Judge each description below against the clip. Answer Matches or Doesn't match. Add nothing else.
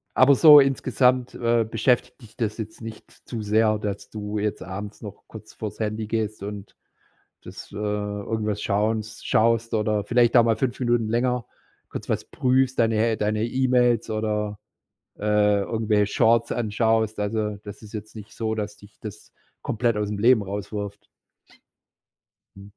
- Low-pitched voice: Matches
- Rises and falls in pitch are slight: Matches